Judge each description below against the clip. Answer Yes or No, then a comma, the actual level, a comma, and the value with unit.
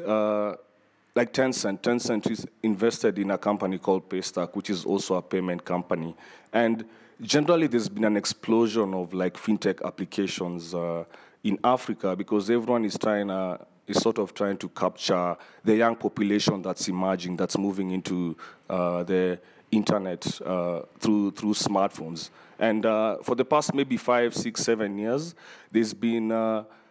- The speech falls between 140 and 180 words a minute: Yes, average, 165 wpm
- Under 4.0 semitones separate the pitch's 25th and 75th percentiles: Yes, average, 3.5 semitones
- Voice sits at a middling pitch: No, low, 105 Hz